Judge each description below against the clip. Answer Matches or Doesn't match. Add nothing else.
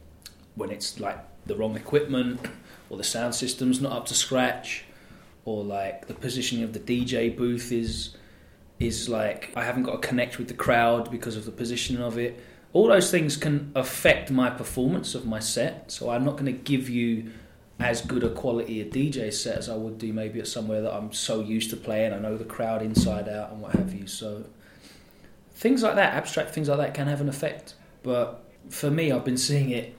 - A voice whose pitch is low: Matches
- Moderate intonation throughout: Matches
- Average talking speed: Doesn't match